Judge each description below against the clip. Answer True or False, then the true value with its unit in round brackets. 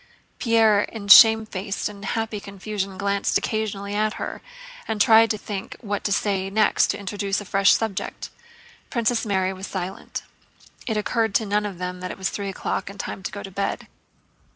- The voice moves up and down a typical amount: False (1.8 semitones)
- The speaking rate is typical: True (180 wpm)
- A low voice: False (200 Hz)